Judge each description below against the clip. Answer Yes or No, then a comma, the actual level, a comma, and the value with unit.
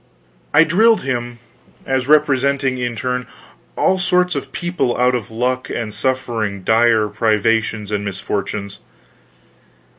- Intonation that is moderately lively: Yes, average, 4.2 semitones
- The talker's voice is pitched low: Yes, low, 125 Hz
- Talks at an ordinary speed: No, slow, 120 wpm